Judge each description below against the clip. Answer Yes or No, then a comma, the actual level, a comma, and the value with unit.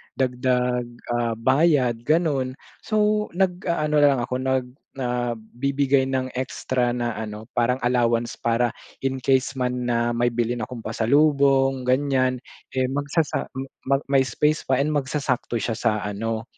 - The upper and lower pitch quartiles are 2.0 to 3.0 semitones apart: Yes, narrow, 2.5 semitones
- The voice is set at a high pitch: No, low, 130 Hz